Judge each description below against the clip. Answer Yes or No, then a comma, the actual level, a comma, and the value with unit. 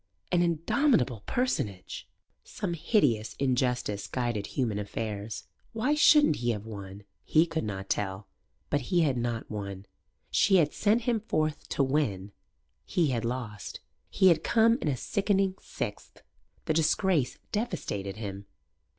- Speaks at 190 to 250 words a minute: No, average, 140 wpm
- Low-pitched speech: Yes, low, 130 Hz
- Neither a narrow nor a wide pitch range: No, wide, 9.0 semitones